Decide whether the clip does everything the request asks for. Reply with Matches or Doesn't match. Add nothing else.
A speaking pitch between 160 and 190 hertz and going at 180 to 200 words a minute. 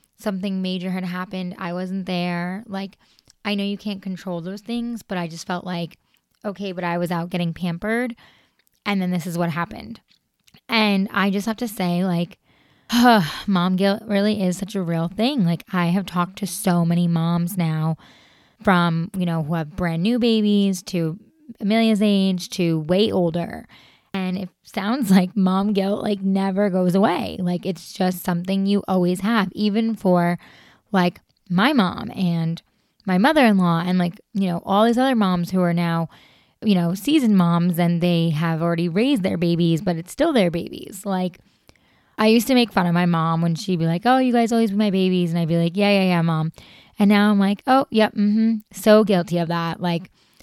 Matches